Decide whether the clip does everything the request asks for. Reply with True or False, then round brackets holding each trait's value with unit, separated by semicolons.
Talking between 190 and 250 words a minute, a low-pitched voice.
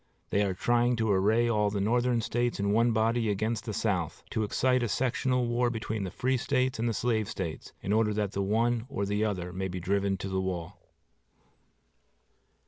True (200 wpm; 110 Hz)